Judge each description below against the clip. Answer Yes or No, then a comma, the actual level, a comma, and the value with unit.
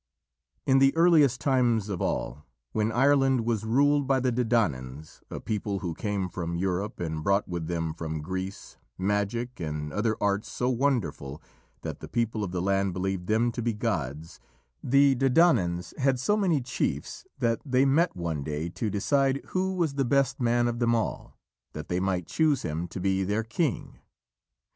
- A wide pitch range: Yes, wide, 6.9 semitones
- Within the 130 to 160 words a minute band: No, average, 175 wpm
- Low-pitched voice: Yes, low, 110 Hz